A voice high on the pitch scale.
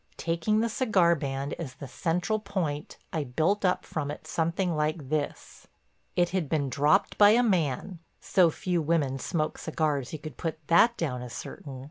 No: medium, 160 Hz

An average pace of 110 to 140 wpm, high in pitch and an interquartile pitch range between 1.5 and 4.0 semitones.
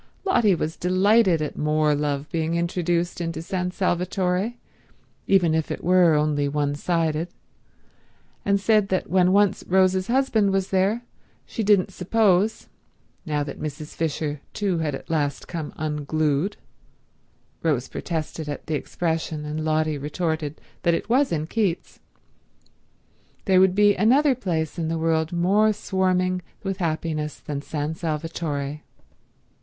No: slow, 135 wpm; medium, 170 Hz; average, 3.7 semitones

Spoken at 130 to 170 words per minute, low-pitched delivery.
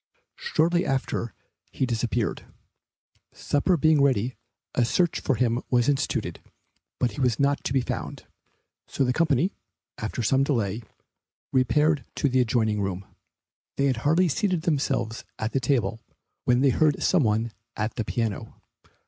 Yes: average, 150 wpm; low, 130 Hz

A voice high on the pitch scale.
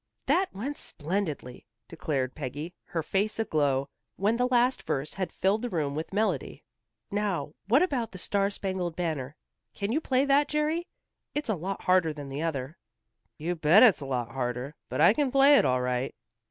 No: medium, 180 Hz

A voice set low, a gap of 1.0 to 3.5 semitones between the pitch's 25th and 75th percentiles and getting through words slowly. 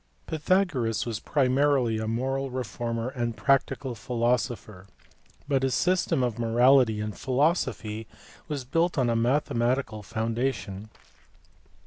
Yes: low, 125 Hz; average, 3.2 semitones; slow, 110 wpm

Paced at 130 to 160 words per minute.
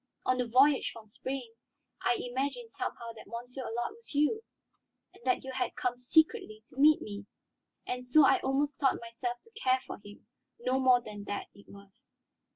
No: average, 175 wpm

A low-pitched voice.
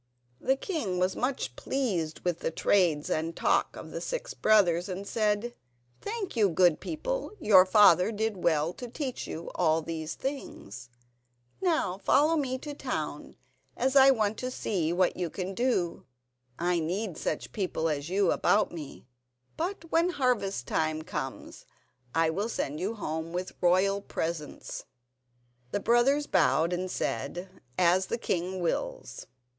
No: high, 190 Hz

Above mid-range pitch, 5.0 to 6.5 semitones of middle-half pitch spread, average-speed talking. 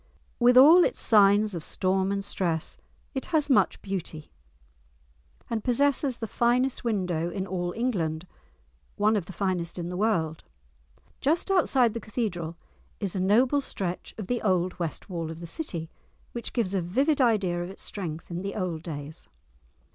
Yes: high, 195 Hz; wide, 5.5 semitones; average, 165 wpm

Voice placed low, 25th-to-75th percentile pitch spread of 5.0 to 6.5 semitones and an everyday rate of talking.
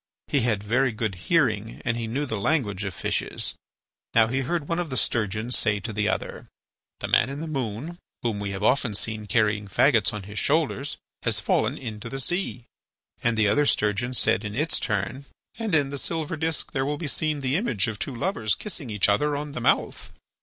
No: low, 120 Hz; wide, 5.5 semitones; fast, 210 wpm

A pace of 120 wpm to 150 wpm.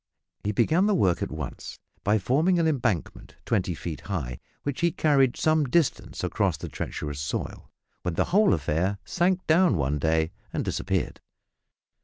No: average, 160 wpm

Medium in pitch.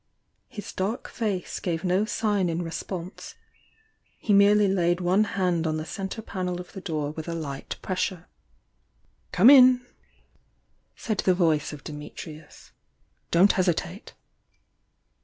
Yes: medium, 180 Hz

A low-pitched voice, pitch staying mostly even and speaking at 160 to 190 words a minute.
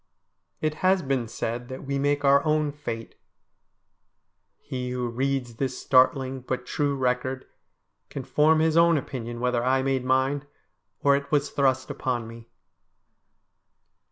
No: low, 130 Hz; narrow, 2.3 semitones; average, 140 wpm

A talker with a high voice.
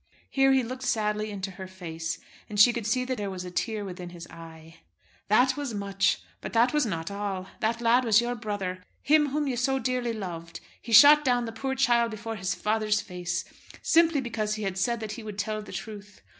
Yes: high, 215 Hz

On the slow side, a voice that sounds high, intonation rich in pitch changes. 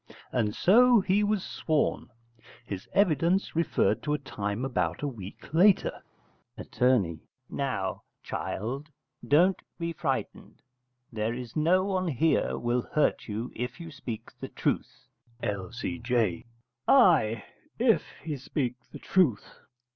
No: slow, 125 wpm; low, 135 Hz; wide, 6.8 semitones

